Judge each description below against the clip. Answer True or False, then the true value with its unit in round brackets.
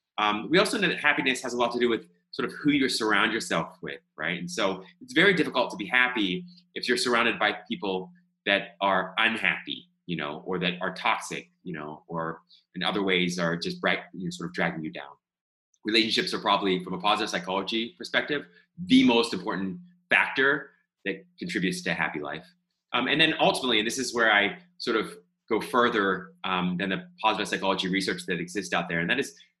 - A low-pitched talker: True (105 Hz)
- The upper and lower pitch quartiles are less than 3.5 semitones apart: False (5.4 semitones)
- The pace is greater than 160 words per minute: True (205 wpm)